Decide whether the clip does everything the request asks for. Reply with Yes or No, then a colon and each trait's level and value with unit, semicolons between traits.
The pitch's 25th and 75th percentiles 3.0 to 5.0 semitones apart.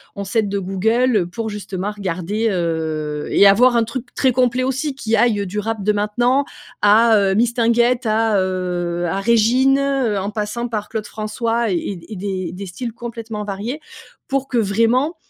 Yes: average, 3.4 semitones